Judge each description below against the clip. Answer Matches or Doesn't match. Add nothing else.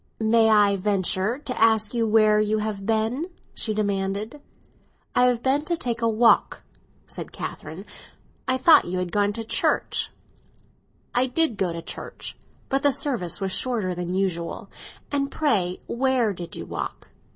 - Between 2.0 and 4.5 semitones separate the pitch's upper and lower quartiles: Matches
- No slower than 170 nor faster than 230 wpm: Doesn't match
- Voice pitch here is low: Doesn't match